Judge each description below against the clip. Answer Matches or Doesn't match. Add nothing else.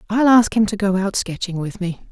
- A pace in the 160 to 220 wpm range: Doesn't match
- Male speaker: Doesn't match